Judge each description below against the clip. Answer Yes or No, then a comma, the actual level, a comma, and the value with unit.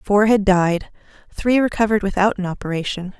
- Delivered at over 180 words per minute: No, average, 150 wpm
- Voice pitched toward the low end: No, high, 200 Hz